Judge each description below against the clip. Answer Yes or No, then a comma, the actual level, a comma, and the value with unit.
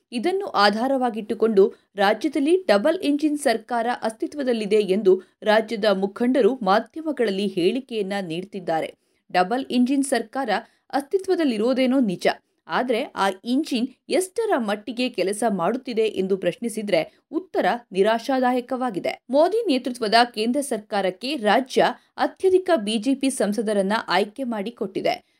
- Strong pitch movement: No, average, 4.7 semitones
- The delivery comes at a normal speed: Yes, average, 90 wpm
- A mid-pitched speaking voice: No, high, 235 Hz